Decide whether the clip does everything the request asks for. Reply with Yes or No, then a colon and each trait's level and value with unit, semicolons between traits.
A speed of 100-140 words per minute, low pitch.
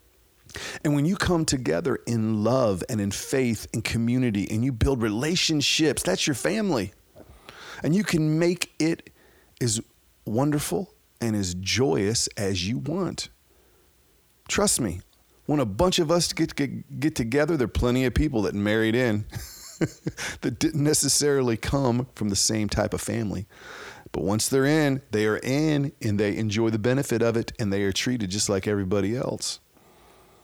No: average, 165 wpm; low, 120 Hz